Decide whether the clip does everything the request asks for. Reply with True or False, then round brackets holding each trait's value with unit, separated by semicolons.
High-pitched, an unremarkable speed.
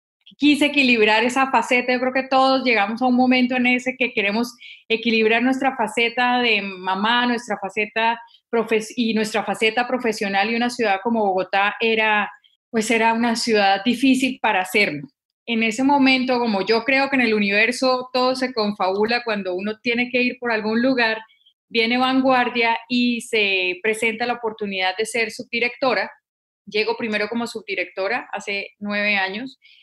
True (230 Hz; 160 wpm)